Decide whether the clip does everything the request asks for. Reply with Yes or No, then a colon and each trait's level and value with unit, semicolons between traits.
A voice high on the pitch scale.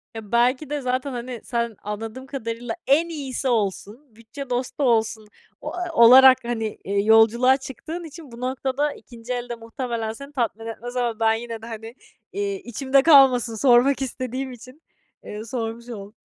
Yes: high, 240 Hz